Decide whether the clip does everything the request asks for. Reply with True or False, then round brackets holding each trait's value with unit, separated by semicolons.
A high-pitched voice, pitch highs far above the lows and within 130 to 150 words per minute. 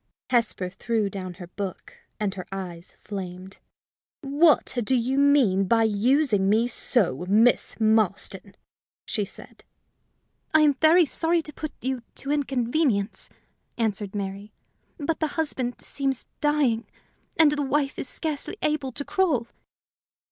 True (240 Hz; 6.3 semitones; 135 wpm)